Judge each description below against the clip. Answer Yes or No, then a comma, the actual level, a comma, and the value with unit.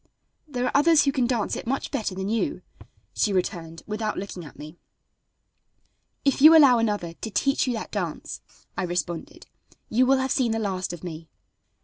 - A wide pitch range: Yes, wide, 6.5 semitones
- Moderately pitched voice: No, high, 220 Hz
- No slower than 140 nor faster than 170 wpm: No, average, 180 wpm